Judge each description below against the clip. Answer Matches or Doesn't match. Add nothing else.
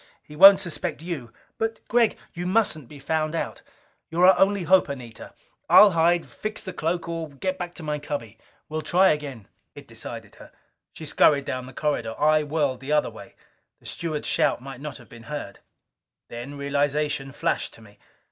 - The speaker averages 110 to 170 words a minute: Doesn't match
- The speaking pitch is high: Doesn't match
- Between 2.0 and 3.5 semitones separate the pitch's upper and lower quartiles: Doesn't match